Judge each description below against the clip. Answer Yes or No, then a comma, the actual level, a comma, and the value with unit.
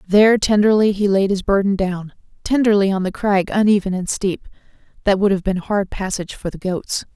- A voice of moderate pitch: No, high, 195 Hz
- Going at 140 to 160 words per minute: No, average, 195 wpm